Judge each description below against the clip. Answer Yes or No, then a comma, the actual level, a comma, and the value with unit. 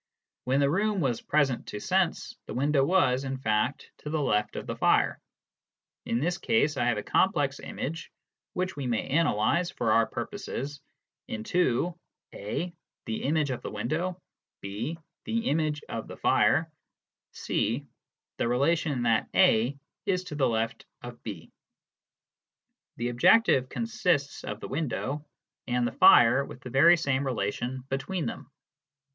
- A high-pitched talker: No, low, 135 Hz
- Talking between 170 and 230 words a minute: No, average, 150 wpm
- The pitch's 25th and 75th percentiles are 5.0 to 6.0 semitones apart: Yes, wide, 5.4 semitones